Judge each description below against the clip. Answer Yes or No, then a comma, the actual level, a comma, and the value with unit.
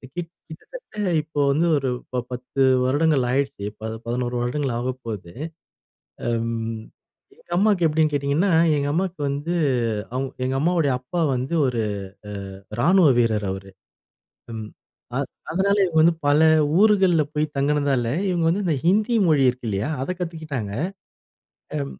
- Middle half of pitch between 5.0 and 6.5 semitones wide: Yes, wide, 5.6 semitones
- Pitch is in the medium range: Yes, medium, 145 Hz